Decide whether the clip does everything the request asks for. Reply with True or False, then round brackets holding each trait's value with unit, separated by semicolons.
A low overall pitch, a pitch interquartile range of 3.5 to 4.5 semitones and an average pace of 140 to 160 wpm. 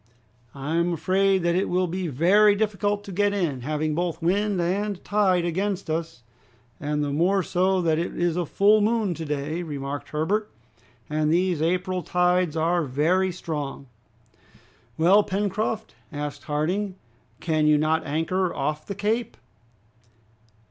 False (175 Hz; 3.9 semitones; 150 wpm)